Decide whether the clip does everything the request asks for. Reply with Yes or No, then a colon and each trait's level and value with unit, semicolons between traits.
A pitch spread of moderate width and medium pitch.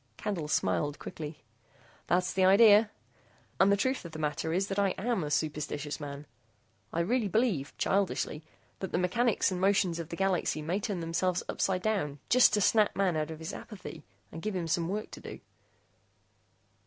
Yes: average, 4.3 semitones; medium, 180 Hz